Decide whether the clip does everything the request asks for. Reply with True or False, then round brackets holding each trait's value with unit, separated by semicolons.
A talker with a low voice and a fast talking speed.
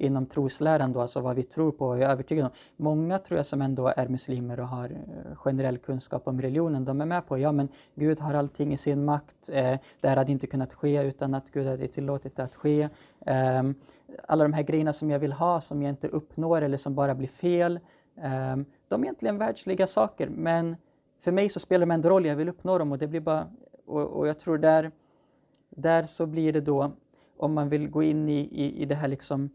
False (145 Hz; 220 wpm)